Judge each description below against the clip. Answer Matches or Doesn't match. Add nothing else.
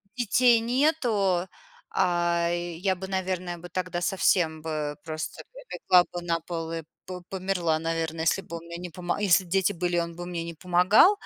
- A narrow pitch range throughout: Matches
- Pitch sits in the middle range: Matches